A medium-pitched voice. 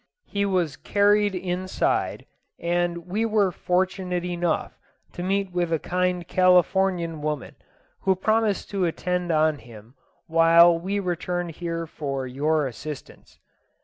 Yes: medium, 175 Hz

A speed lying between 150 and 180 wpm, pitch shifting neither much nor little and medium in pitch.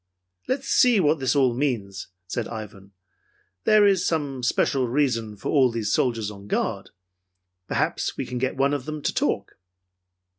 No: average, 160 wpm; average, 4.8 semitones; low, 130 Hz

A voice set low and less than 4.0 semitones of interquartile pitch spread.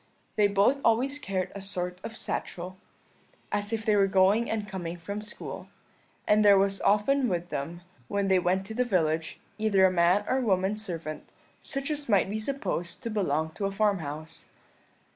No: high, 195 Hz; average, 3.2 semitones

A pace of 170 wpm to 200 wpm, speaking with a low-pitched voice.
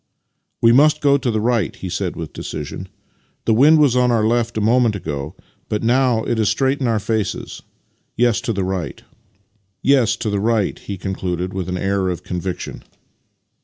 Yes: average, 175 wpm; low, 110 Hz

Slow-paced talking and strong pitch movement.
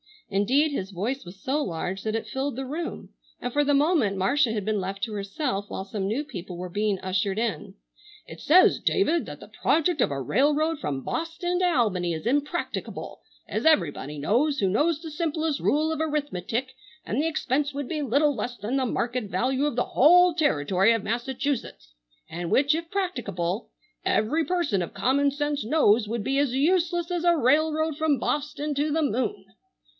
No: average, 185 wpm; wide, 6.9 semitones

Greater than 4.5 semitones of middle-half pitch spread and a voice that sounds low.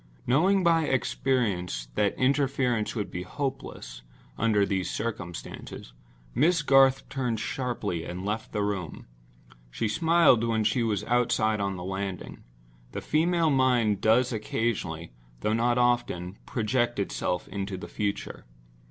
Yes: average, 5.1 semitones; low, 110 Hz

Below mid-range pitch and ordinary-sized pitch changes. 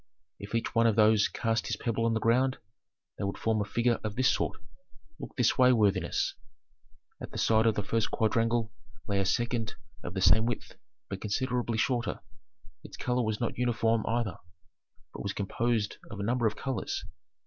No: low, 115 Hz; narrow, 2.1 semitones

